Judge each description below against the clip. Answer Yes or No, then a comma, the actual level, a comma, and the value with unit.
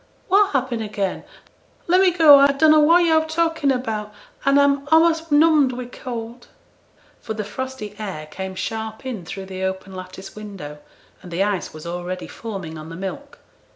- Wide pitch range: Yes, wide, 7.2 semitones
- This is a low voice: No, high, 225 Hz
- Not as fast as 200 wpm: Yes, average, 170 wpm